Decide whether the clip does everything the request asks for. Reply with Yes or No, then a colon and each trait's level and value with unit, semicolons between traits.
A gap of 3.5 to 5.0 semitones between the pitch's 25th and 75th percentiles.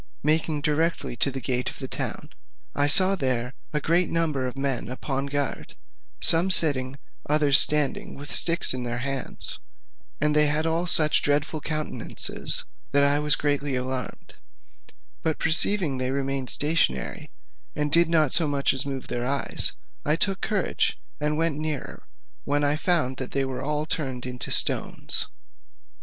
No: average, 2.8 semitones